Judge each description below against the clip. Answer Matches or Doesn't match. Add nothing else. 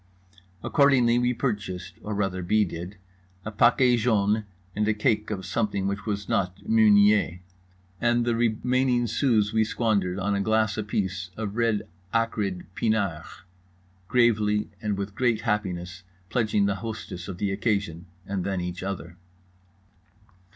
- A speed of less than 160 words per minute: Matches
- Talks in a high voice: Doesn't match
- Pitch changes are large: Doesn't match